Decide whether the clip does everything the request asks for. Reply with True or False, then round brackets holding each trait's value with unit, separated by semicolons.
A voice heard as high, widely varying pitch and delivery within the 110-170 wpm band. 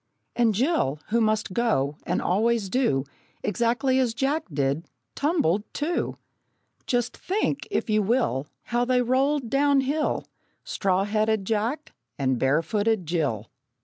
True (225 Hz; 6.2 semitones; 135 wpm)